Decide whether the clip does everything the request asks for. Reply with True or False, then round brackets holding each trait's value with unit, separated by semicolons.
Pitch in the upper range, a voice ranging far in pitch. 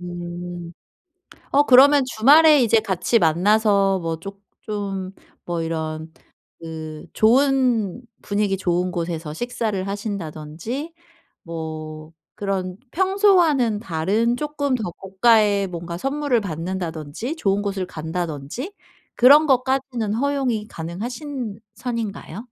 True (200 Hz; 6.4 semitones)